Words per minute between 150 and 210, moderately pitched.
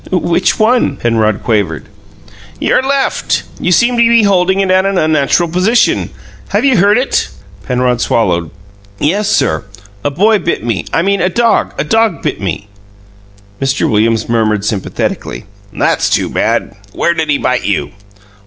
Yes: average, 155 wpm; medium, 165 Hz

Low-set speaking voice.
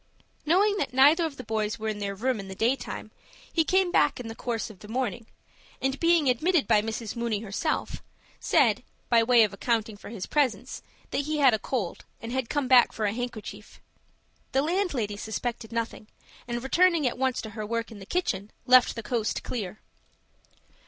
No: high, 240 Hz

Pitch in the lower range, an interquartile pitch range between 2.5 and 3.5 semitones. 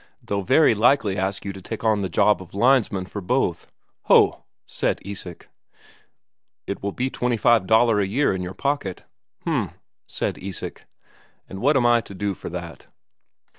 No: low, 100 Hz; average, 4.0 semitones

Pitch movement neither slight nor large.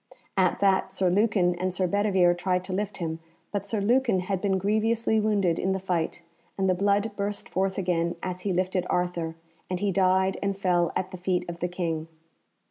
No: narrow, 2.1 semitones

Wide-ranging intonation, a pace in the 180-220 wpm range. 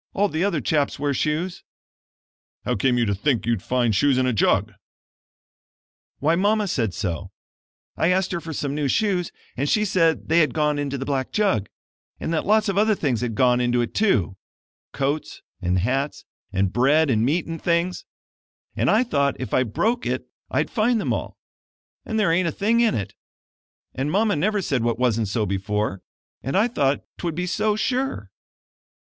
Yes: wide, 7.6 semitones; average, 190 wpm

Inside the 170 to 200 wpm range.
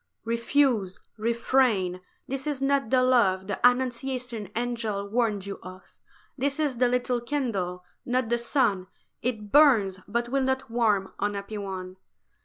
No: average, 145 wpm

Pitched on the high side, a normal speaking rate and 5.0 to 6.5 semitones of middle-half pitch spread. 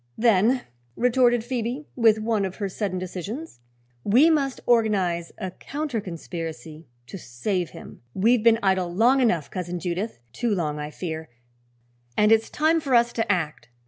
Yes: high, 210 Hz; average, 155 wpm; average, 5.3 semitones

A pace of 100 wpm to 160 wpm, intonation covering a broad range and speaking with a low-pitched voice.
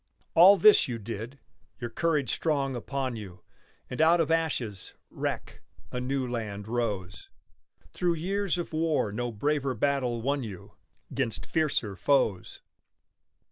Yes: slow, 135 wpm; wide, 5.9 semitones; low, 130 Hz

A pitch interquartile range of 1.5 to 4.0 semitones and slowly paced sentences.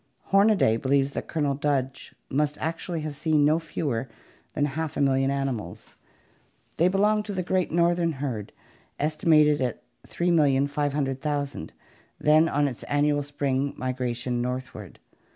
Yes: average, 3.0 semitones; slow, 130 wpm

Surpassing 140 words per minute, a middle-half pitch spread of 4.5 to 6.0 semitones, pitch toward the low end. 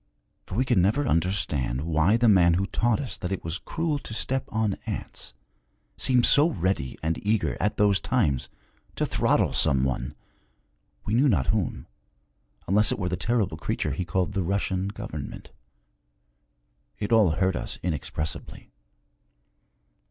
Yes: average, 150 wpm; average, 5.1 semitones; very low, 95 Hz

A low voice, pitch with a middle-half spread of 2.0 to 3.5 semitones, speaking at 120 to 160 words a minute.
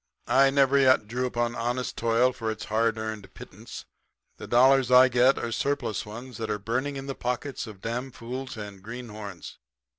No: low, 120 Hz; average, 2.9 semitones; average, 170 wpm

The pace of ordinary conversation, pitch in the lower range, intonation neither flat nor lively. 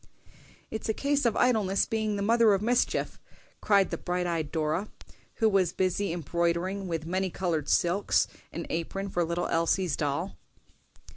No: average, 155 wpm; medium, 185 Hz; average, 3.4 semitones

